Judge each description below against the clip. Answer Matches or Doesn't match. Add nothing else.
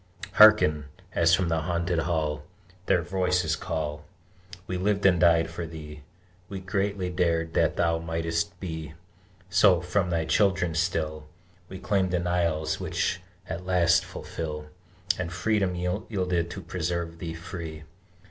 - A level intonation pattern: Matches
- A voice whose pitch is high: Doesn't match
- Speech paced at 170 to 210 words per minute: Doesn't match